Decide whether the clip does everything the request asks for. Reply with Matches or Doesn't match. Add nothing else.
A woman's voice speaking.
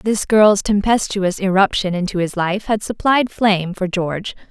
Matches